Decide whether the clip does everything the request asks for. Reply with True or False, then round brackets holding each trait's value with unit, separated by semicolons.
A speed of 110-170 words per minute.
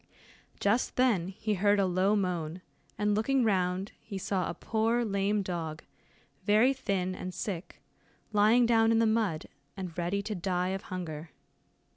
True (155 wpm)